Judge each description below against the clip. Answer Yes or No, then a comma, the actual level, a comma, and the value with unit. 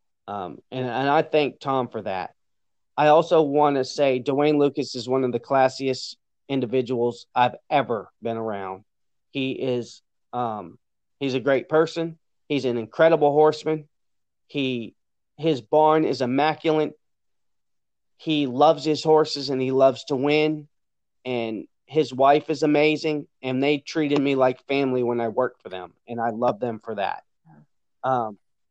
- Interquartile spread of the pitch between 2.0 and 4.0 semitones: Yes, average, 3.5 semitones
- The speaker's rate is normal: Yes, average, 160 wpm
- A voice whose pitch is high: No, low, 135 Hz